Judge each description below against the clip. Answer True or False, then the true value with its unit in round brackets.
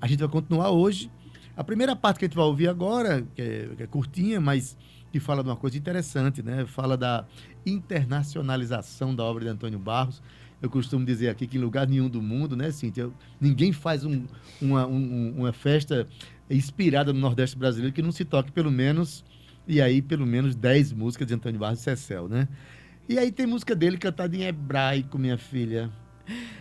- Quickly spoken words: True (195 wpm)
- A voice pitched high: False (135 Hz)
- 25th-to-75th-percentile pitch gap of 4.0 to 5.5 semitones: True (4.3 semitones)